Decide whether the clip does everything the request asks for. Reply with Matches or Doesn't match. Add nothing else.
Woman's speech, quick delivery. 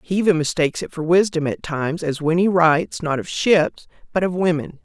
Matches